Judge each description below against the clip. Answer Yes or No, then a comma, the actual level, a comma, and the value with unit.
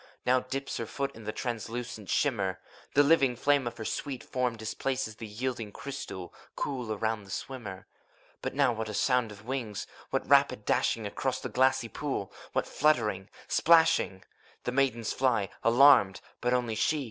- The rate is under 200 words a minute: Yes, average, 160 wpm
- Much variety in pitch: No, average, 3.8 semitones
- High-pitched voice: No, low, 120 Hz